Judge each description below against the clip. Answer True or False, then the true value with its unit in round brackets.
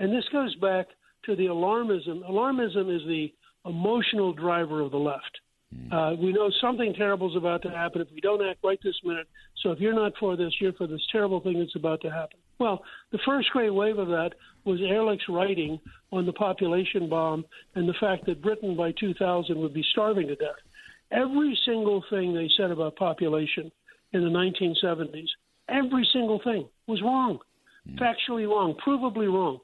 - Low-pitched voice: False (190 Hz)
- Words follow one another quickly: False (185 wpm)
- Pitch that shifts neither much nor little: True (4.1 semitones)